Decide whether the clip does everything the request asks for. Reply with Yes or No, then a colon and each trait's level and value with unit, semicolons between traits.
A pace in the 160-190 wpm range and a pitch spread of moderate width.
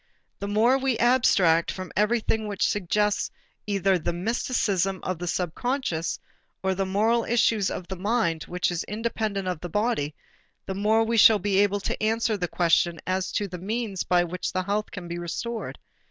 Yes: average, 175 wpm; average, 3.7 semitones